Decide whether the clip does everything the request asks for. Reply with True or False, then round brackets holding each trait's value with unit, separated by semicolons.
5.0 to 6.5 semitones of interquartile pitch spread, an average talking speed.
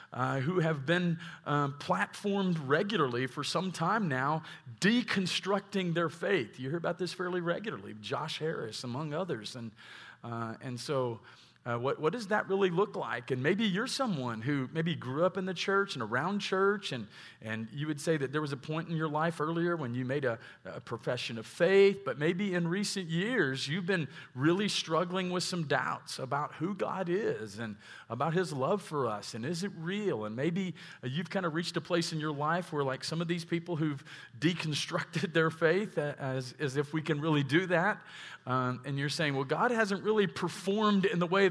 False (5.3 semitones; 210 wpm)